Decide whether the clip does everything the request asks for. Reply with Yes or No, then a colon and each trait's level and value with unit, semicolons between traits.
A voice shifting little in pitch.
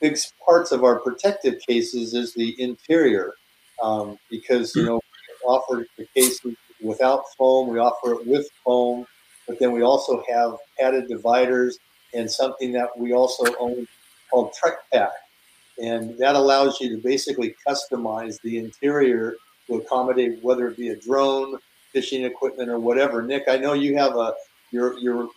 Yes: narrow, 2.3 semitones